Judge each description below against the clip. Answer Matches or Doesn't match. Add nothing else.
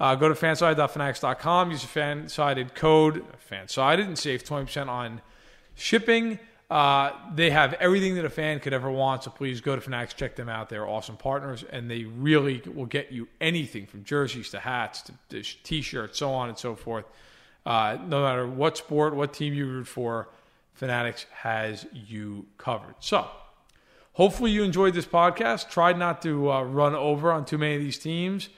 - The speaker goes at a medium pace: Matches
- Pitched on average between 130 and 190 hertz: Matches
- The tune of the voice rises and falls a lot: Doesn't match